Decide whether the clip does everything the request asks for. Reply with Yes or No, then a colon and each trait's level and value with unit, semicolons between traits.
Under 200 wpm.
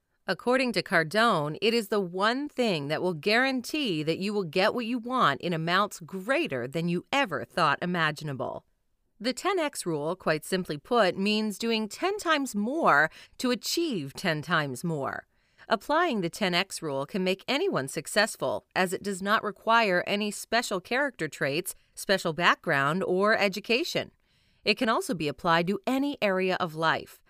Yes: average, 160 wpm